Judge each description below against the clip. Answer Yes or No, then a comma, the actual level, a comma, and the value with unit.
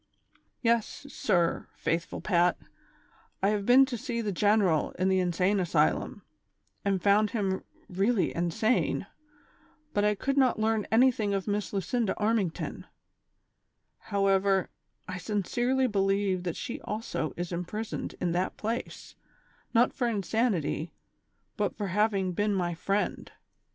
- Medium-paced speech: No, slow, 130 wpm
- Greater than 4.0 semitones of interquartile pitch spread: No, average, 3.4 semitones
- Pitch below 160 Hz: No, high, 200 Hz